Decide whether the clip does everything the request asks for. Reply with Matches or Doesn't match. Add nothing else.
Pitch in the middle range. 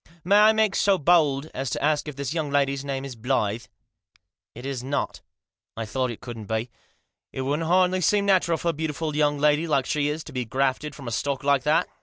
Matches